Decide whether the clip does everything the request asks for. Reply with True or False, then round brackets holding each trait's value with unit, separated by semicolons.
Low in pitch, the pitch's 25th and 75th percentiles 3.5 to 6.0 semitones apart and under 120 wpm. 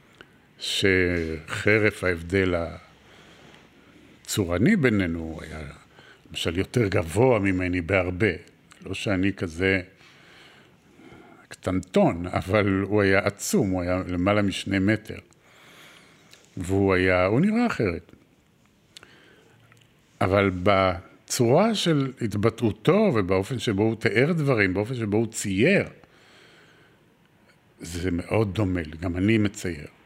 False (95 Hz; 3.0 semitones; 100 wpm)